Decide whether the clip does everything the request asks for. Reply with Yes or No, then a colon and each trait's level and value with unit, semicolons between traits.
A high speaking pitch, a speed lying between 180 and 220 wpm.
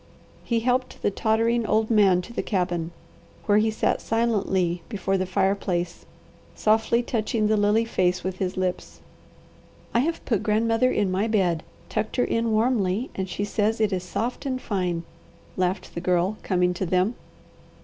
No: high, 205 Hz; average, 165 wpm